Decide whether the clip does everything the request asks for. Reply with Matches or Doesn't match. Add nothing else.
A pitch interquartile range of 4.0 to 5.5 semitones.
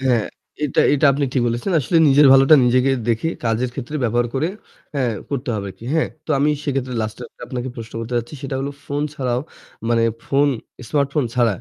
Doesn't match